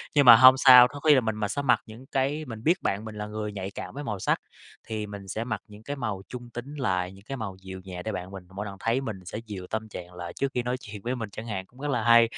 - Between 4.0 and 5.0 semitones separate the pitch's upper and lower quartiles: Yes, average, 4.3 semitones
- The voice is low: Yes, low, 110 Hz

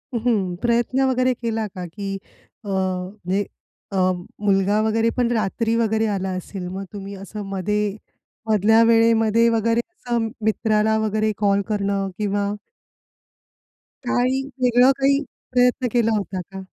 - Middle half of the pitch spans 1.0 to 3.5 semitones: Yes, average, 2.8 semitones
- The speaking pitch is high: Yes, high, 215 Hz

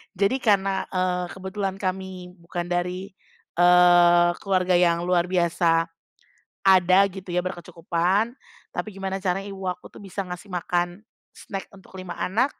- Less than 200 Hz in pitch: Yes, medium, 185 Hz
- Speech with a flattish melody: Yes, narrow, 1.6 semitones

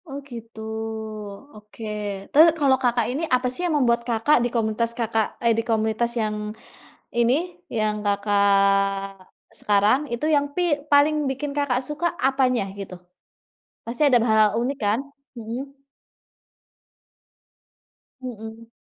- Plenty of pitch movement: No, average, 4.0 semitones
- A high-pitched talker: Yes, high, 235 Hz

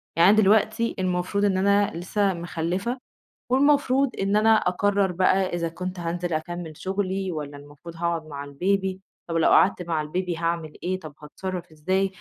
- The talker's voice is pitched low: No, medium, 185 Hz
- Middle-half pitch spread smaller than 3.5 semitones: Yes, average, 3.0 semitones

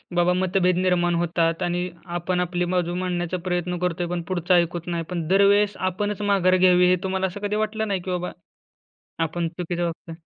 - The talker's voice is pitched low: No, medium, 180 Hz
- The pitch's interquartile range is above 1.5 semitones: No, narrow, 1.2 semitones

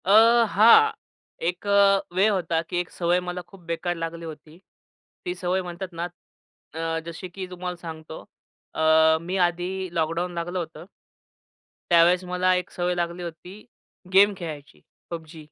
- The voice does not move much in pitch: Yes, narrow, 1.8 semitones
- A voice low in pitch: No, medium, 175 Hz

